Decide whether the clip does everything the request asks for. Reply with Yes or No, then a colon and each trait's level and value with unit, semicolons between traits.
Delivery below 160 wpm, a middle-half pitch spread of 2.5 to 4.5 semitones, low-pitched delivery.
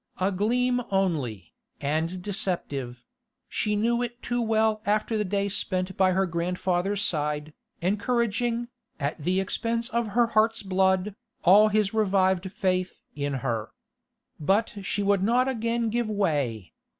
No: average, 140 wpm; average, 3.8 semitones; high, 195 Hz